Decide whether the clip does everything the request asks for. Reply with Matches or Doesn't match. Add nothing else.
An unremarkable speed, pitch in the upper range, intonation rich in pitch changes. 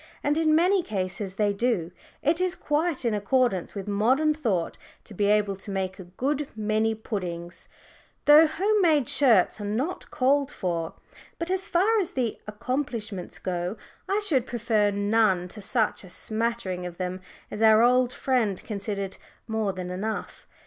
Matches